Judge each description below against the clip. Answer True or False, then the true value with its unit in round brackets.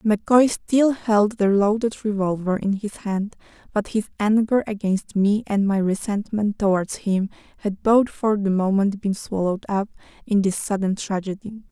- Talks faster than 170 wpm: False (160 wpm)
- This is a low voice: False (205 Hz)